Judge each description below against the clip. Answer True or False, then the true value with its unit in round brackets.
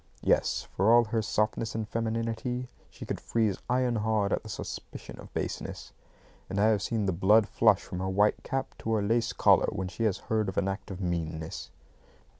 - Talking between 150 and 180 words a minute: False (200 wpm)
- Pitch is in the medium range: False (110 Hz)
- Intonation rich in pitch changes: False (2.9 semitones)